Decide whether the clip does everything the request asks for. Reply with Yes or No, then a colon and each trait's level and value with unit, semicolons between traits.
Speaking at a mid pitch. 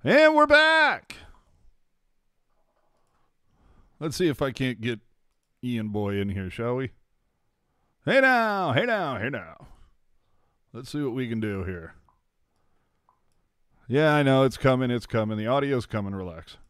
No: low, 125 Hz